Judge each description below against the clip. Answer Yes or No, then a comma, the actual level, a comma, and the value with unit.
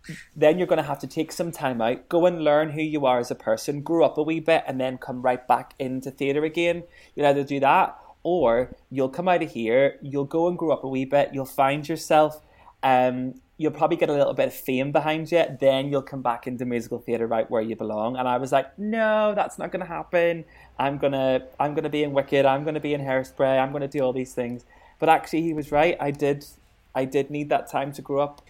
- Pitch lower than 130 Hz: No, medium, 140 Hz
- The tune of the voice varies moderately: Yes, average, 3.3 semitones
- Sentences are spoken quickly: Yes, fast, 250 wpm